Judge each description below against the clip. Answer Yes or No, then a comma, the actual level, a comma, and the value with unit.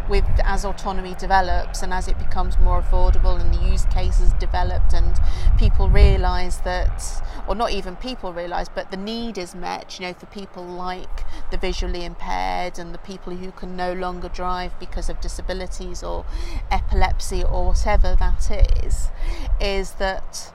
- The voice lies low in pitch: No, medium, 175 Hz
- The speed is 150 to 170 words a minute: Yes, average, 165 wpm